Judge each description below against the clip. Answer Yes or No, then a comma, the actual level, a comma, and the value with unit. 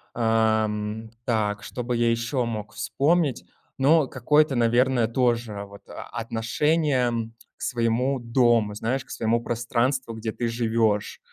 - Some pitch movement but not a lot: No, narrow, 2.3 semitones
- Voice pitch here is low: Yes, low, 115 Hz